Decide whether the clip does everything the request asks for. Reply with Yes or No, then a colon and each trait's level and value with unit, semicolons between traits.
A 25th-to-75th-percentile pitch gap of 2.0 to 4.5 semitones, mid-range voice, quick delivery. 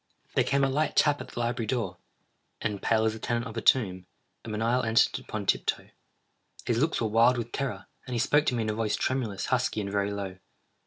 No: average, 3.0 semitones; low, 115 Hz; fast, 220 wpm